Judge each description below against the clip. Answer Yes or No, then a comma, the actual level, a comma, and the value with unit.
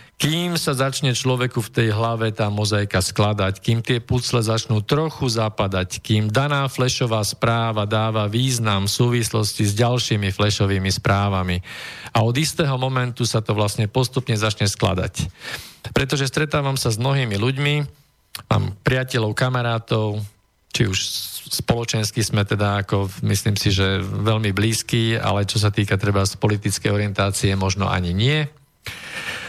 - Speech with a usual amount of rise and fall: Yes, average, 3.5 semitones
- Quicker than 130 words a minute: Yes, average, 140 wpm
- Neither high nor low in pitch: No, low, 110 Hz